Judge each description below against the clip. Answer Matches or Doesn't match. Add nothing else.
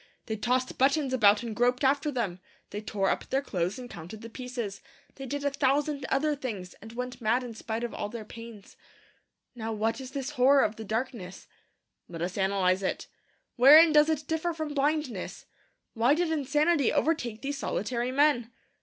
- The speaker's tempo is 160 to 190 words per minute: Matches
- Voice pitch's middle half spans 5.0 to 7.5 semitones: Doesn't match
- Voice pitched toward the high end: Matches